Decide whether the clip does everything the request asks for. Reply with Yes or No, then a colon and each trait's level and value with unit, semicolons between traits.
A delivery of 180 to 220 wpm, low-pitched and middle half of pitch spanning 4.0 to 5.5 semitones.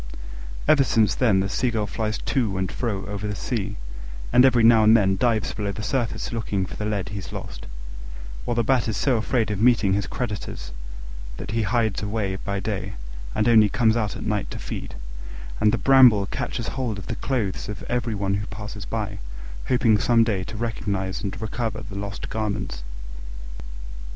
No: average, 185 wpm; low, 105 Hz; average, 2.7 semitones